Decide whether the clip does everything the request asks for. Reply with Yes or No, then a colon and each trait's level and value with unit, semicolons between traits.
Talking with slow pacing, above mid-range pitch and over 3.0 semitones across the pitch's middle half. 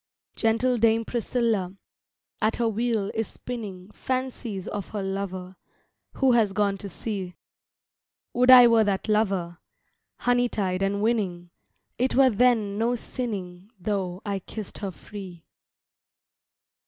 Yes: slow, 130 wpm; high, 210 Hz; average, 3.4 semitones